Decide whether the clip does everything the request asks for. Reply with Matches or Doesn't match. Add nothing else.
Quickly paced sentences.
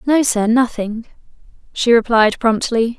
Doesn't match